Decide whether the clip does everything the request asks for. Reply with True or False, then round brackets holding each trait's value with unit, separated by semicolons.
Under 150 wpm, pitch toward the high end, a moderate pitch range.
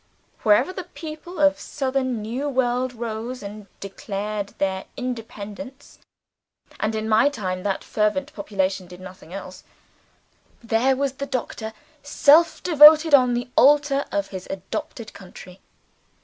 False (135 wpm; 240 Hz; 5.8 semitones)